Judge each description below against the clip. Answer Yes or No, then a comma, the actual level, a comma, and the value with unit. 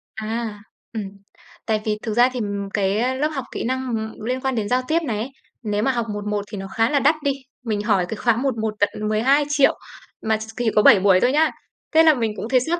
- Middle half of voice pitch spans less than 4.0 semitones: Yes, average, 3.5 semitones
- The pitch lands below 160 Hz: No, high, 230 Hz